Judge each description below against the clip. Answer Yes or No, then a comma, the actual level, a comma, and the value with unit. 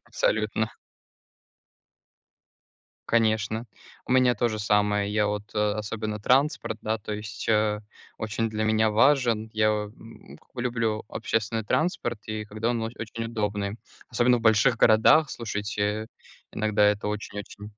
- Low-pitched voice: Yes, low, 110 Hz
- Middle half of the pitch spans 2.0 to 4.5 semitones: No, narrow, 1.5 semitones